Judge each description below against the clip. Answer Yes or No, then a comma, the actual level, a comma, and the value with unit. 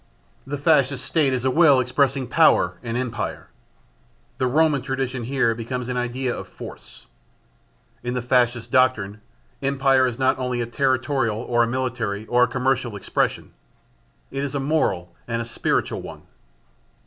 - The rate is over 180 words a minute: No, average, 155 wpm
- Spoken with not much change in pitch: Yes, narrow, 2.2 semitones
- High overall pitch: No, low, 125 Hz